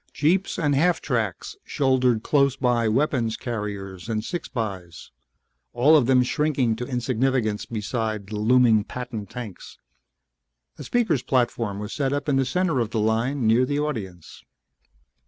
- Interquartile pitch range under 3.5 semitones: No, average, 4.1 semitones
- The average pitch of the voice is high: No, low, 125 Hz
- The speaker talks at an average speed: Yes, average, 150 wpm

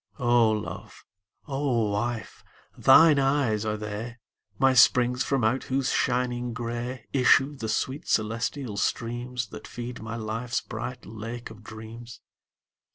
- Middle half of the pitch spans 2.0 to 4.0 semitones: Yes, narrow, 2.4 semitones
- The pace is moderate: No, slow, 130 wpm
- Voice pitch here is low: Yes, low, 120 Hz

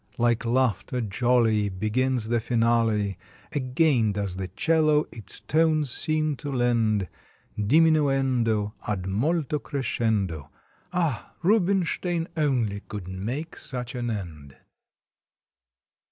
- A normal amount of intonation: No, wide, 6.0 semitones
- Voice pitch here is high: No, low, 120 Hz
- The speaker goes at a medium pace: No, slow, 100 wpm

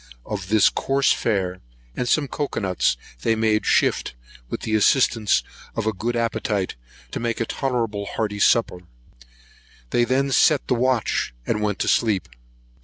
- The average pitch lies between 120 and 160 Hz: No, low, 110 Hz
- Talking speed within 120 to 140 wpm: No, average, 155 wpm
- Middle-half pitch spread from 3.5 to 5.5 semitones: No, average, 2.9 semitones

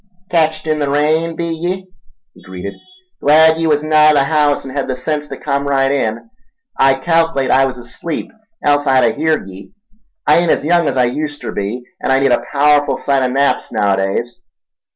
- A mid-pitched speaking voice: Yes, medium, 145 Hz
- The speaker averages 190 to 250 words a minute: Yes, average, 195 wpm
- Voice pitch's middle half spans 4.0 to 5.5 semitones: No, average, 3.2 semitones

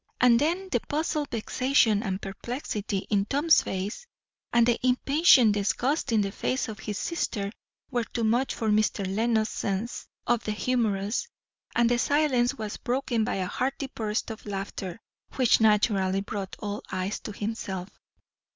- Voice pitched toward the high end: Yes, high, 225 Hz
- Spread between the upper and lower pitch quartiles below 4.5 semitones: Yes, average, 3.8 semitones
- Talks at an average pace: Yes, average, 155 wpm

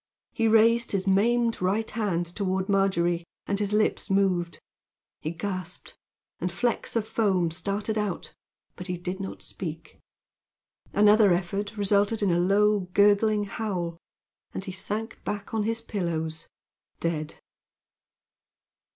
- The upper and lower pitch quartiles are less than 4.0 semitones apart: Yes, average, 2.9 semitones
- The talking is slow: Yes, slow, 130 wpm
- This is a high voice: Yes, high, 200 Hz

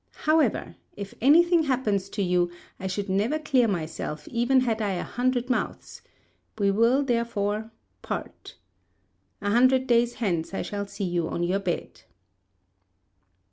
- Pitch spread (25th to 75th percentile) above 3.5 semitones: Yes, average, 4.6 semitones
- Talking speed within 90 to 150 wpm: Yes, average, 145 wpm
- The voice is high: Yes, high, 220 Hz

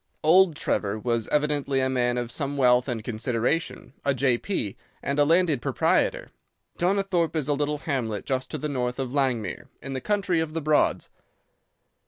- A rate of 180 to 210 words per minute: No, average, 170 wpm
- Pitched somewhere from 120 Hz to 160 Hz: Yes, medium, 140 Hz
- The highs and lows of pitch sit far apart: No, average, 3.9 semitones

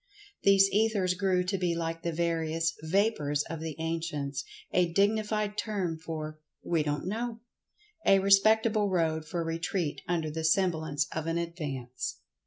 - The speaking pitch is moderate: Yes, medium, 170 Hz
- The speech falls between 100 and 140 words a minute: Yes, slow, 135 wpm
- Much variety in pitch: No, average, 3.7 semitones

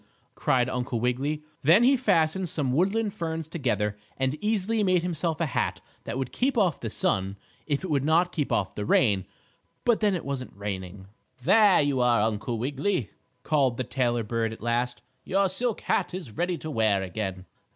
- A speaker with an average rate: Yes, average, 180 wpm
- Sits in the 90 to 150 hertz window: Yes, medium, 140 Hz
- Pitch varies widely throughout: Yes, wide, 7.7 semitones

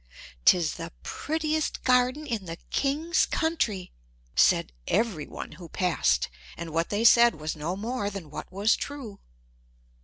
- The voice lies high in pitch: Yes, high, 205 Hz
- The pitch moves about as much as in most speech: No, wide, 7.3 semitones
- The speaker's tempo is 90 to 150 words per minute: Yes, average, 145 wpm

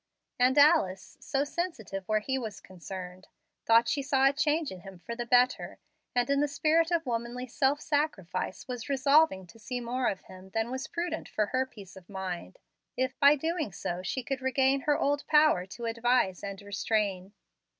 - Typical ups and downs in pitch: No, wide, 6.0 semitones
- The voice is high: Yes, very high, 250 Hz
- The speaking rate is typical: Yes, average, 185 wpm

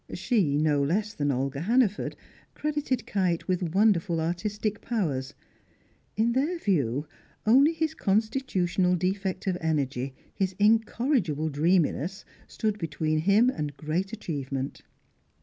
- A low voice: No, medium, 185 Hz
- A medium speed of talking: No, slow, 115 wpm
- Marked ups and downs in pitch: Yes, wide, 6.0 semitones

